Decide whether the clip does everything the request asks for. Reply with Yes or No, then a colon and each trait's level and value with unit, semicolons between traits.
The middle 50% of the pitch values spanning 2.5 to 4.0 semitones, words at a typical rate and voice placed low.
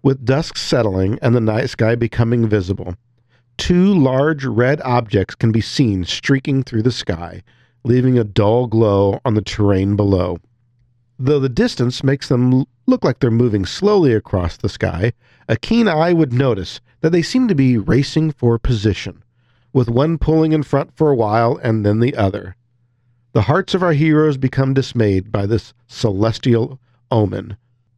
Yes: average, 3.5 semitones; average, 165 wpm; low, 120 Hz